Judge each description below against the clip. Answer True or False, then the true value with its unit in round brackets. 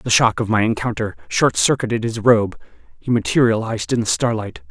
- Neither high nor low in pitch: False (110 Hz)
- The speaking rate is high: False (180 wpm)